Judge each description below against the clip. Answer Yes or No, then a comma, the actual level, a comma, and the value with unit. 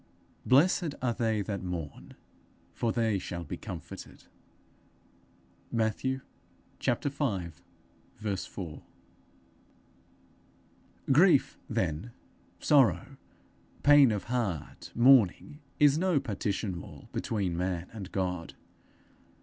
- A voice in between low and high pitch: No, low, 110 Hz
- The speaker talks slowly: Yes, slow, 90 wpm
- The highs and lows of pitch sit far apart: Yes, wide, 6.5 semitones